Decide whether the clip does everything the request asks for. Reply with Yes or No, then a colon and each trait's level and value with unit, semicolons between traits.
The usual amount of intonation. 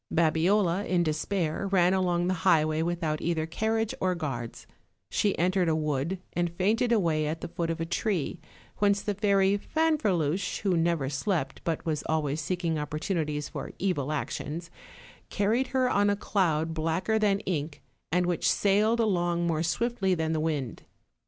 Yes: average, 4.0 semitones